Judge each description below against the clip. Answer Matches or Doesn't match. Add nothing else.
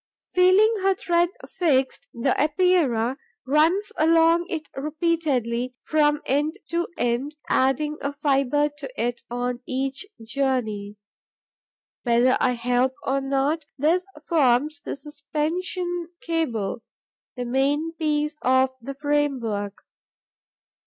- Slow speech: Matches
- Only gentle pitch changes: Doesn't match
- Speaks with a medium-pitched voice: Doesn't match